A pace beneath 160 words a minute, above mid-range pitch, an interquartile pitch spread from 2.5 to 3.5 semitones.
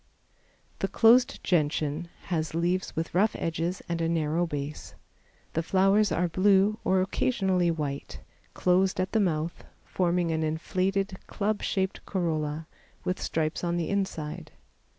No: slow, 135 wpm; medium, 175 Hz; average, 3.0 semitones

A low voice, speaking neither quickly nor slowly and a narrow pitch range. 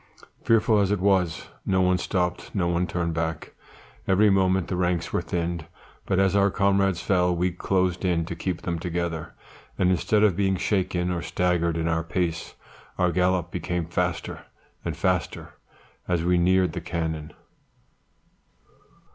Yes: very low, 90 Hz; average, 155 wpm; narrow, 1.7 semitones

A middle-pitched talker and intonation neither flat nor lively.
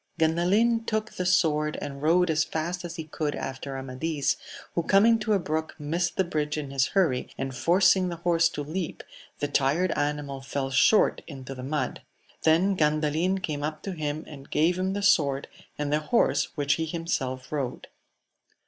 Yes: medium, 155 Hz; average, 3.8 semitones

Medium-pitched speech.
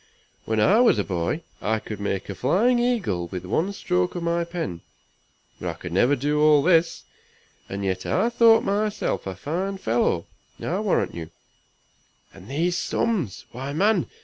Yes: medium, 150 Hz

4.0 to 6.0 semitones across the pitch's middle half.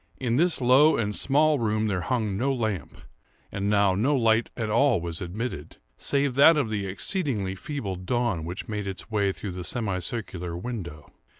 Yes: average, 5.0 semitones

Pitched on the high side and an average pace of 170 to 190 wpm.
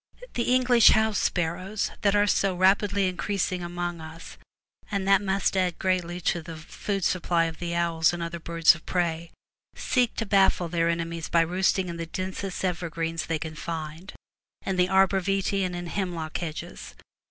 No: medium, 175 Hz; average, 175 wpm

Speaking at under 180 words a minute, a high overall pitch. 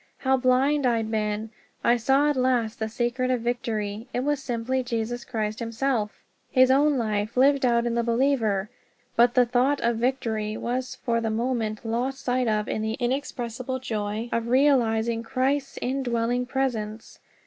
Yes: average, 160 wpm; high, 240 Hz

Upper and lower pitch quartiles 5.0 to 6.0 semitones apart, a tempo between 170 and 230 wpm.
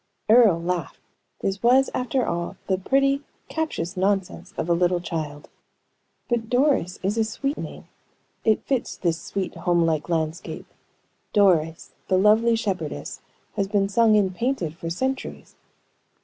No: wide, 5.4 semitones; average, 140 wpm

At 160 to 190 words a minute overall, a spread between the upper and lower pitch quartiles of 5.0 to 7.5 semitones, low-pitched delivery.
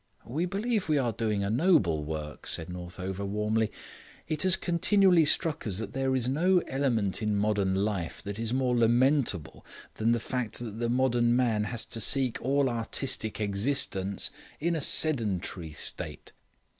Yes: average, 165 wpm; average, 5.3 semitones; low, 115 Hz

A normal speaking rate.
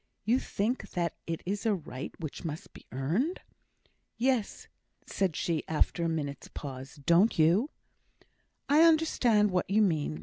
Yes: average, 145 wpm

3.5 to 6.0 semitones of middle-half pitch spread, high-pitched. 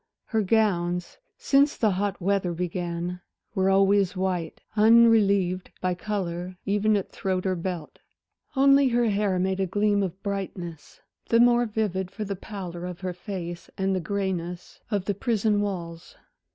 No: average, 2.7 semitones; high, 195 Hz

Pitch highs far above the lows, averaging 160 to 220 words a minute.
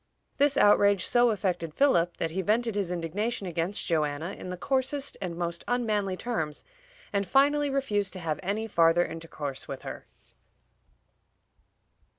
No: wide, 5.8 semitones; average, 145 wpm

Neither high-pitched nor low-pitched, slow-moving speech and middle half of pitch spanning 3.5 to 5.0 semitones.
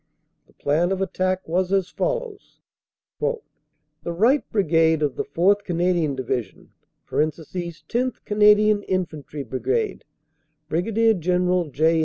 Yes: medium, 180 Hz; slow, 110 wpm; average, 4.3 semitones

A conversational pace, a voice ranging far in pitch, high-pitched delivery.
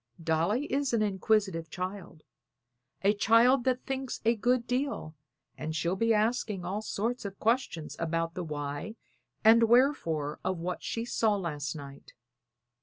Yes: average, 145 wpm; wide, 6.0 semitones; high, 205 Hz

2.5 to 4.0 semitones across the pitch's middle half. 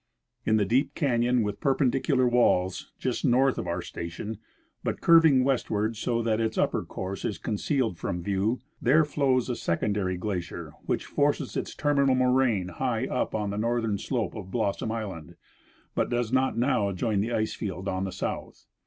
No: average, 4.6 semitones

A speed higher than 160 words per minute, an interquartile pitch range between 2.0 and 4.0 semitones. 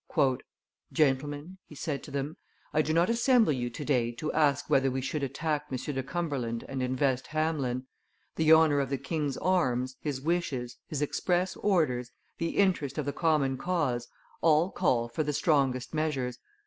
Yes: average, 170 wpm; average, 3.6 semitones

